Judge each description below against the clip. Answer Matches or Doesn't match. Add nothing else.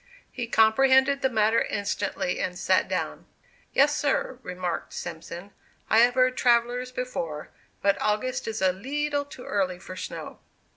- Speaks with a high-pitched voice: Matches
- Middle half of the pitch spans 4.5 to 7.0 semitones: Matches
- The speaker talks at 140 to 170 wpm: Matches